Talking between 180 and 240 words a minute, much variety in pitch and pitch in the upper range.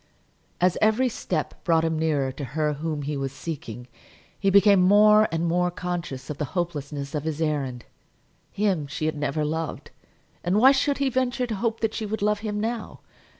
No: average, 190 wpm; wide, 6.1 semitones; medium, 170 Hz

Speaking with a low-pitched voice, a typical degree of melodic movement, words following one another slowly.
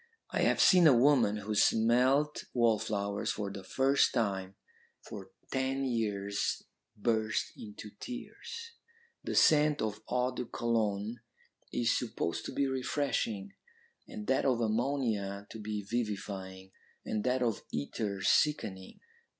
Yes: low, 110 Hz; average, 4.4 semitones; slow, 125 wpm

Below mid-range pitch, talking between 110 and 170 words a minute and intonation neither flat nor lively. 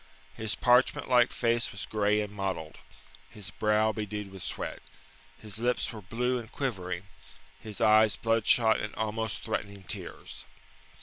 No: low, 110 Hz; average, 140 wpm; narrow, 2.0 semitones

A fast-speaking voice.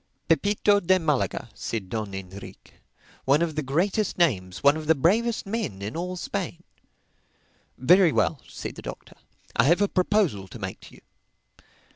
No: average, 160 wpm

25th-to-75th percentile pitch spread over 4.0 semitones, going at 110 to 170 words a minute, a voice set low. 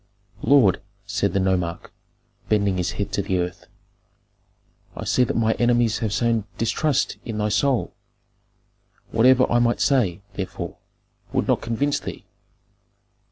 No: average, 3.5 semitones; slow, 135 wpm; low, 110 Hz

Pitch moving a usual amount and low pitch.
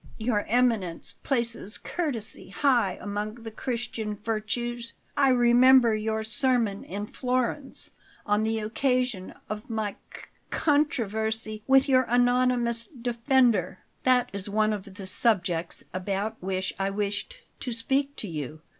No: average, 3.3 semitones; high, 225 Hz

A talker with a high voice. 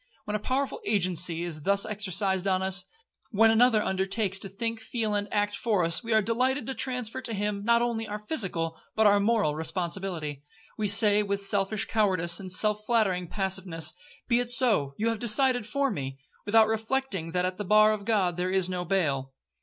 Yes: high, 205 Hz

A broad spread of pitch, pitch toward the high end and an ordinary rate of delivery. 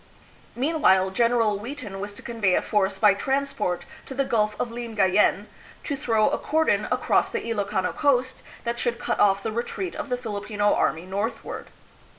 No: average, 3.7 semitones; high, 220 Hz; average, 175 wpm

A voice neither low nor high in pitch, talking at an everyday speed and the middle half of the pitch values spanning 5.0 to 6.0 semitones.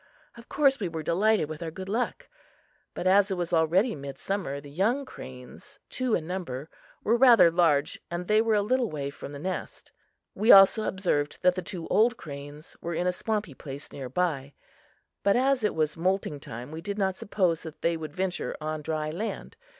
Yes: medium, 180 Hz; average, 195 wpm; average, 5.3 semitones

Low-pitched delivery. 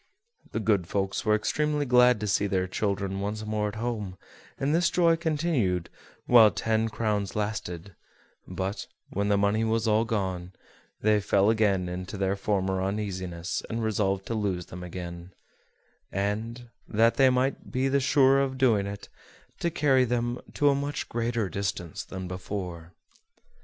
Yes: low, 105 Hz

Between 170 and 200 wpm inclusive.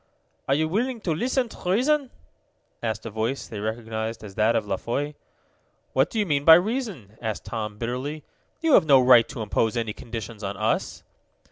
Yes: average, 190 wpm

